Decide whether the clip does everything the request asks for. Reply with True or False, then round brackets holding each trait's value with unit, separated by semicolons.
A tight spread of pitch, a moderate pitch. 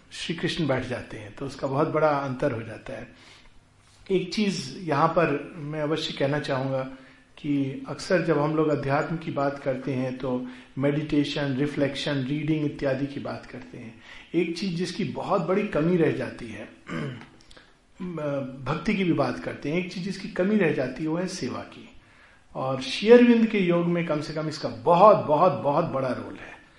False (4.3 semitones; 150 Hz)